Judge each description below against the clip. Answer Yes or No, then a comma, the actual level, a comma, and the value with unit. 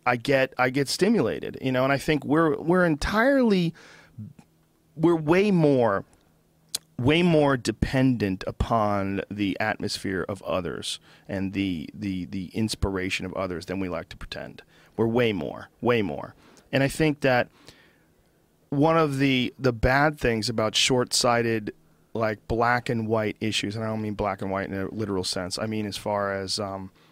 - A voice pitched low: Yes, low, 115 Hz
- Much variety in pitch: Yes, wide, 6.0 semitones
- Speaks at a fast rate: No, average, 170 wpm